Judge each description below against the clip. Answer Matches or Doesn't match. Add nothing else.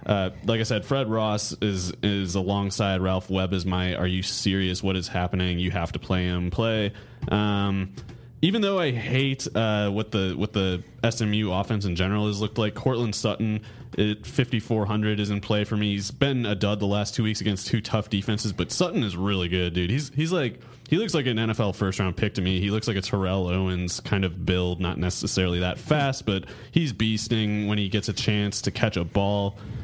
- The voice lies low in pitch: Matches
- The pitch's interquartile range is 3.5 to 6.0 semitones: Doesn't match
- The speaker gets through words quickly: Matches